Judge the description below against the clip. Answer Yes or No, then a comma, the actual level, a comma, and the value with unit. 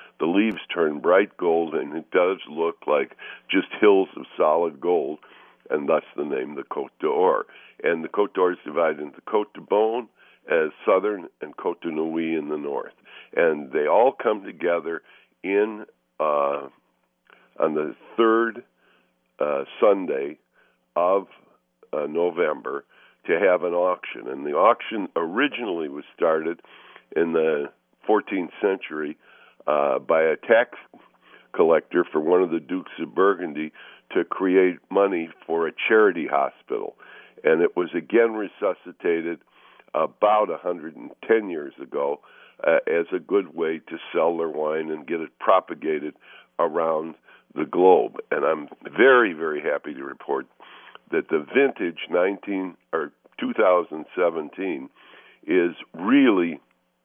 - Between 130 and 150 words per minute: Yes, average, 145 wpm